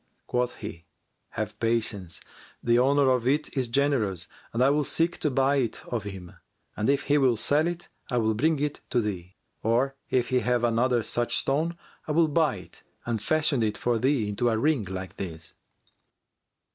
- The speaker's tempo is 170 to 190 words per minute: Yes, average, 185 wpm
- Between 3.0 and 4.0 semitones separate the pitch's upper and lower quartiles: No, average, 4.7 semitones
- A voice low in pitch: Yes, low, 120 Hz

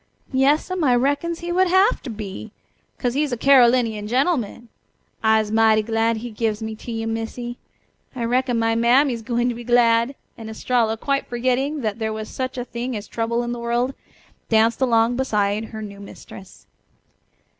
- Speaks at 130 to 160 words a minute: No, average, 170 wpm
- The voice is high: Yes, high, 235 Hz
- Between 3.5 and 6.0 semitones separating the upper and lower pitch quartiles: No, narrow, 2.6 semitones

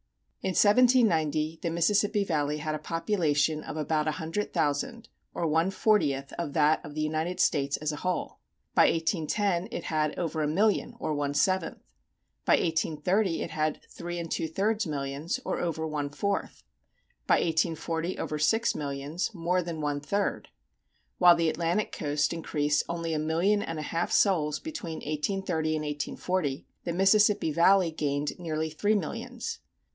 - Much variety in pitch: No, average, 3.3 semitones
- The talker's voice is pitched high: No, medium, 160 Hz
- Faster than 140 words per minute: Yes, average, 160 wpm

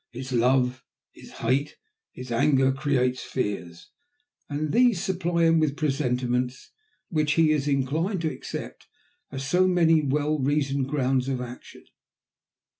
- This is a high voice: No, medium, 140 Hz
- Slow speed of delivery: Yes, slow, 130 wpm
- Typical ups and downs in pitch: Yes, average, 3.4 semitones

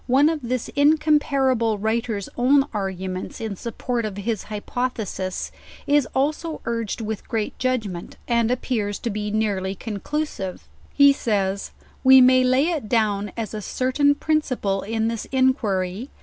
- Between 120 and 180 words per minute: Yes, average, 145 wpm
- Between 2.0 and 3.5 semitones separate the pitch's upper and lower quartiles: No, average, 4.2 semitones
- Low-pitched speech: No, high, 230 Hz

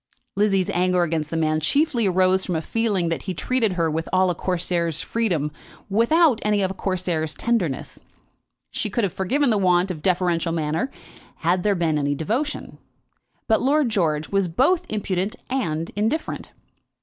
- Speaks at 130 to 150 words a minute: No, average, 165 wpm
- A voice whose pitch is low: No, medium, 185 Hz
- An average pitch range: Yes, average, 4.9 semitones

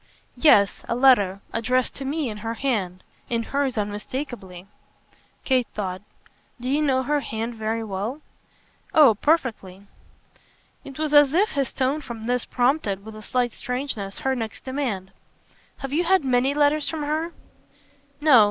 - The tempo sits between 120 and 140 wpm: No, average, 150 wpm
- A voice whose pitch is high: Yes, very high, 250 Hz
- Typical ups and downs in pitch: Yes, average, 4.7 semitones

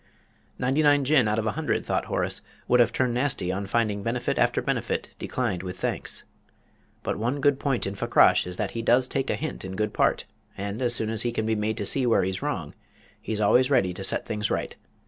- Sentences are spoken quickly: Yes, fast, 225 wpm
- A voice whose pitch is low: Yes, low, 115 Hz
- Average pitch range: Yes, average, 4.1 semitones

